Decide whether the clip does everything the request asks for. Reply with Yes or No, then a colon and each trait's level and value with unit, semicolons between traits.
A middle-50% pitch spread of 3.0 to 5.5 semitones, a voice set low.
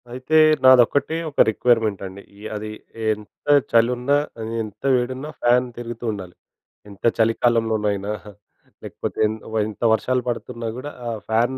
No: narrow, 2.6 semitones; low, 115 Hz